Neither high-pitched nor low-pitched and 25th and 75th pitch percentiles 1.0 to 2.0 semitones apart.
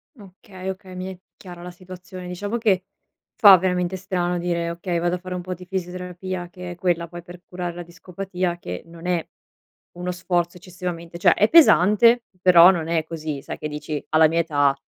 Yes: medium, 180 Hz; narrow, 1.4 semitones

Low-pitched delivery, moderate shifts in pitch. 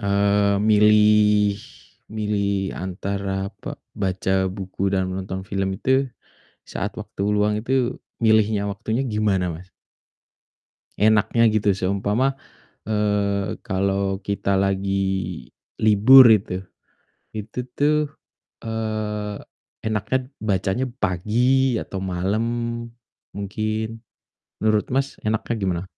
No: low, 105 Hz; narrow, 2.0 semitones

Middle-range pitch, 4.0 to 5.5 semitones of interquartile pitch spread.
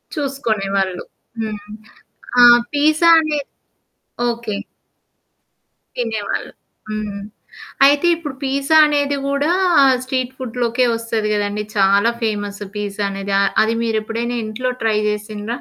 No: high, 225 Hz; average, 4.5 semitones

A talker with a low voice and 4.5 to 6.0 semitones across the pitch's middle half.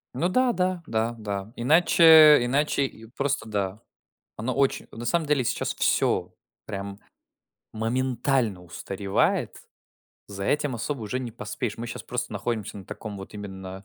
Yes: low, 115 Hz; average, 5.3 semitones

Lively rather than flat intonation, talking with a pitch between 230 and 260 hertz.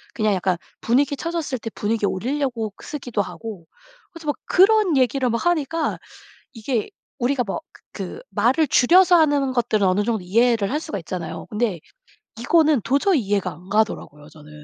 Yes: wide, 6.2 semitones; high, 240 Hz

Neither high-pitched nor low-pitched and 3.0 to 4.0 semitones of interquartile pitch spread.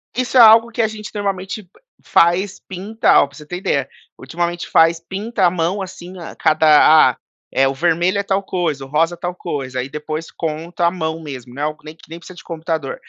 Yes: medium, 170 Hz; average, 3.7 semitones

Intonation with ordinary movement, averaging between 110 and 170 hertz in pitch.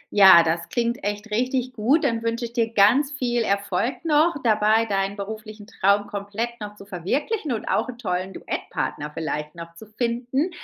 No: average, 3.5 semitones; high, 220 Hz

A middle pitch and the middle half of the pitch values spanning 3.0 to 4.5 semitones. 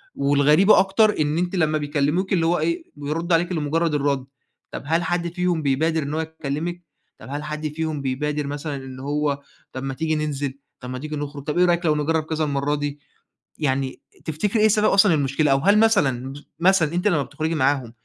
Yes: medium, 150 Hz; average, 3.3 semitones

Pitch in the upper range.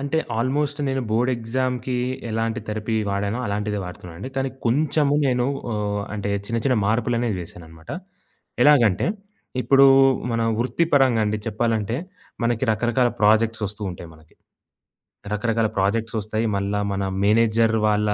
No: low, 115 Hz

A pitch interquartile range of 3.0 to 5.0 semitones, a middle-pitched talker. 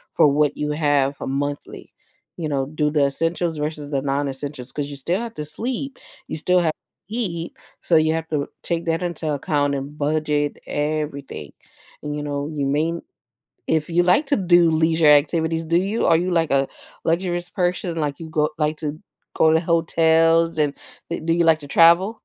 No: narrow, 2.5 semitones; medium, 155 Hz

